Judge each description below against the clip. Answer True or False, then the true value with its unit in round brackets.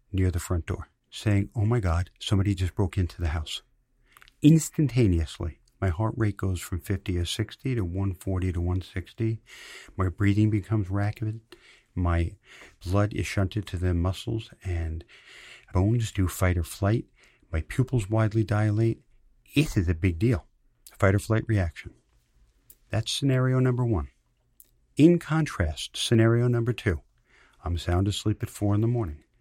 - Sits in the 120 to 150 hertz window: False (100 Hz)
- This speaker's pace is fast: False (150 wpm)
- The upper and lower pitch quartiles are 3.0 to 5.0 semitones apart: True (4.0 semitones)